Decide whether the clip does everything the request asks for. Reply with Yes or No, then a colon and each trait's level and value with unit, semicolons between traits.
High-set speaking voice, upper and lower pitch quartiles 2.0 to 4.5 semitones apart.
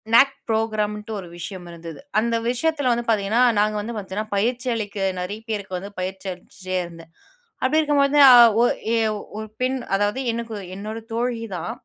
Yes: high, 215 Hz; average, 3.8 semitones